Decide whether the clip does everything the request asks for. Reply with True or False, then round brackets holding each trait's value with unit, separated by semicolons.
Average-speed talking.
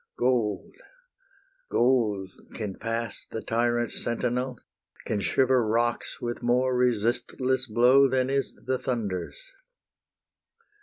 False (100 wpm)